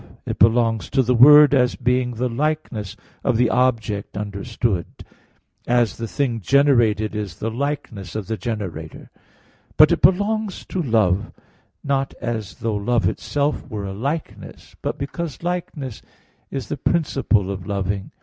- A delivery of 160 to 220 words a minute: No, average, 145 wpm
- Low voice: Yes, low, 120 Hz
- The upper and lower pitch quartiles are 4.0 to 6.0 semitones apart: Yes, average, 4.9 semitones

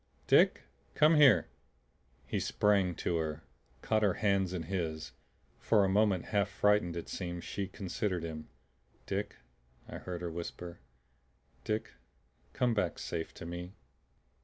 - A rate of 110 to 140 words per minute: Yes, slow, 135 wpm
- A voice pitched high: No, very low, 90 Hz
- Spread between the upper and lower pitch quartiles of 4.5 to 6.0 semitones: No, average, 3.3 semitones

